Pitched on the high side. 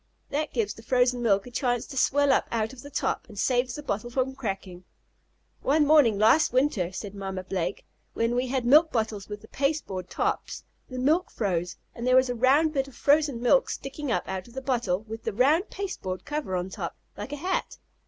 Yes: high, 245 Hz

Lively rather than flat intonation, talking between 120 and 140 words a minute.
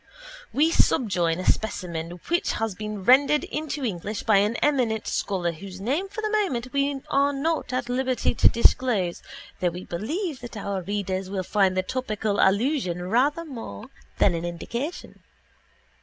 No: wide, 6.8 semitones; average, 155 wpm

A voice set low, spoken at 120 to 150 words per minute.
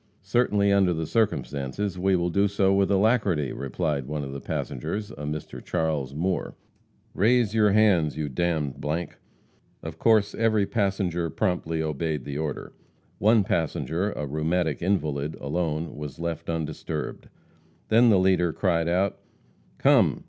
Yes: very low, 85 Hz; average, 145 wpm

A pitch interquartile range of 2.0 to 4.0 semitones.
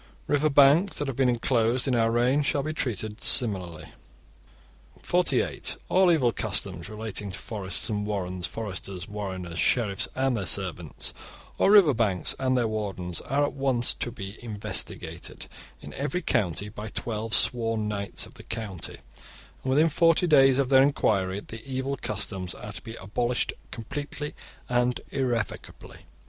No: average, 4.9 semitones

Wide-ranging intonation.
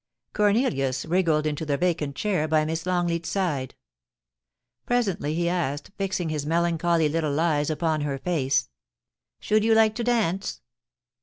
No: average, 3.8 semitones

